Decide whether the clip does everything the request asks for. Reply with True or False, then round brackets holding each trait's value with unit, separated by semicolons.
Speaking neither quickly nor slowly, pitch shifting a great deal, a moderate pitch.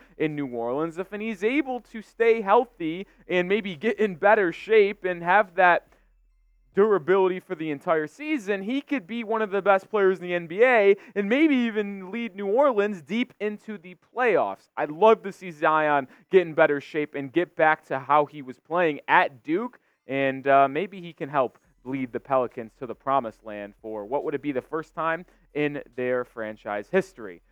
True (190 wpm; 6.6 semitones; 175 Hz)